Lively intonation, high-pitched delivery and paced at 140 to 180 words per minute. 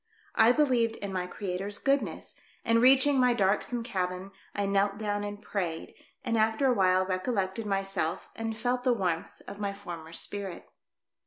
No: average, 3.5 semitones; high, 205 Hz; average, 160 wpm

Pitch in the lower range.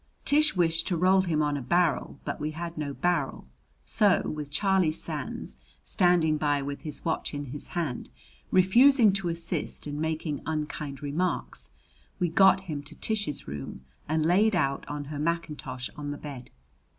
No: medium, 155 Hz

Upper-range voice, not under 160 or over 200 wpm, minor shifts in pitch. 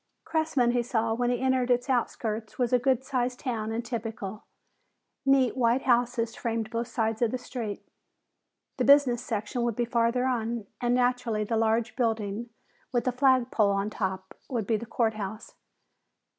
Yes: high, 235 Hz; average, 170 wpm; narrow, 2.0 semitones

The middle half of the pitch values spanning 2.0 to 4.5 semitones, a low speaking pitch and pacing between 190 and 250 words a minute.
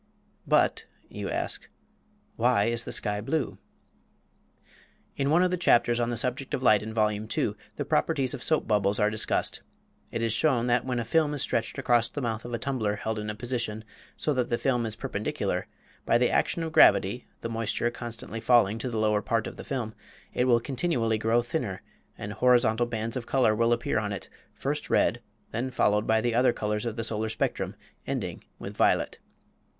Yes: narrow, 2.4 semitones; low, 115 Hz; average, 195 wpm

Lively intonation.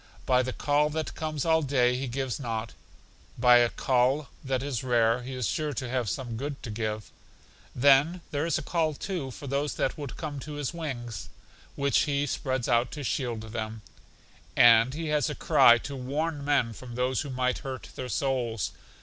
No: average, 3.1 semitones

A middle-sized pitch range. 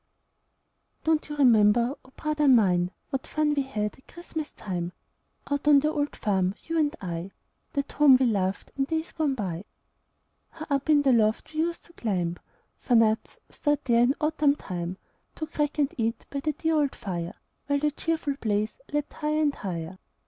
No: wide, 6.4 semitones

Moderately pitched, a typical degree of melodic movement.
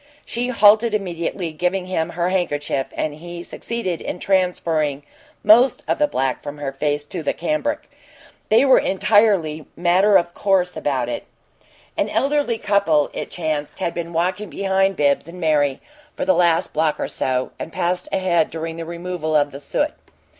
Yes: medium, 175 Hz; average, 4.4 semitones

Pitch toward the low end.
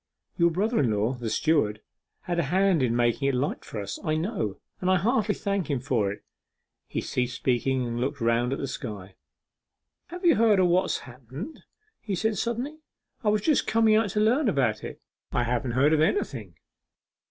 No: medium, 145 Hz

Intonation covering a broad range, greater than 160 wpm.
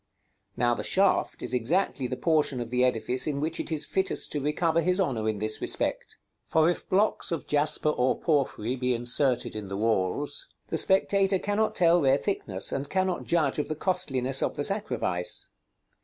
Yes: wide, 6.1 semitones; average, 185 wpm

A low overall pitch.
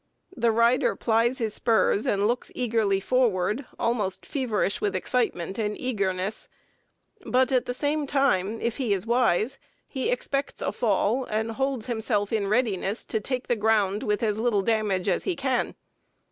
No: high, 225 Hz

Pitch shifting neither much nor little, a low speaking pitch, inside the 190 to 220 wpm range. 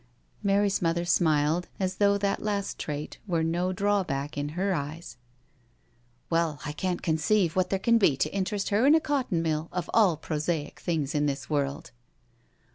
No: average, 4.7 semitones; medium, 170 Hz; average, 195 wpm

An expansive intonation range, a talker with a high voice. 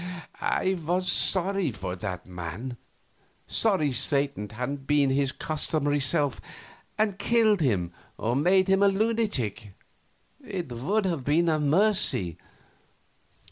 No: wide, 7.7 semitones; medium, 145 Hz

